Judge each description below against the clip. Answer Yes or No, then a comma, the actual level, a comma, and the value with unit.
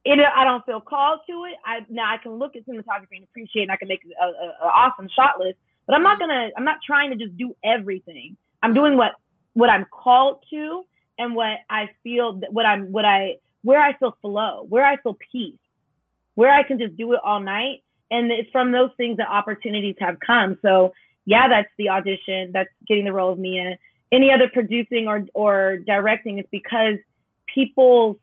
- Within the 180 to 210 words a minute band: Yes, fast, 205 wpm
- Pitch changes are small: No, average, 4.1 semitones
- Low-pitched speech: No, high, 225 Hz